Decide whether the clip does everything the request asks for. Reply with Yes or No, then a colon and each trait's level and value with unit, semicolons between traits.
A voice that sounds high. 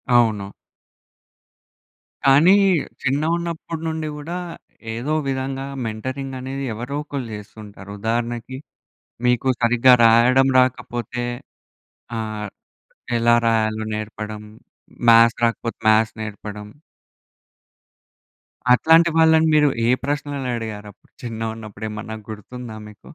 No: low, 120 Hz